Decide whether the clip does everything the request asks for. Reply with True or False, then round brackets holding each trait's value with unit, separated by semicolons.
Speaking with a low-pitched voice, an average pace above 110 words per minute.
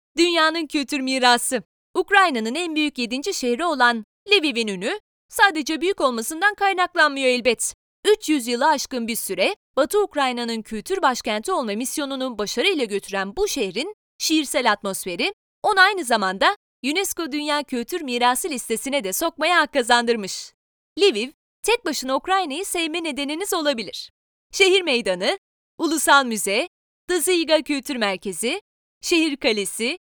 False (290 Hz; 120 wpm)